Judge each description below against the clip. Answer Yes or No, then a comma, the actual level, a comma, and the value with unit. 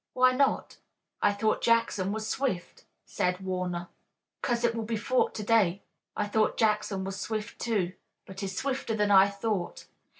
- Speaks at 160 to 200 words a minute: Yes, average, 165 wpm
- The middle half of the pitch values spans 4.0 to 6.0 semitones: No, average, 3.2 semitones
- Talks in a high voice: Yes, high, 210 Hz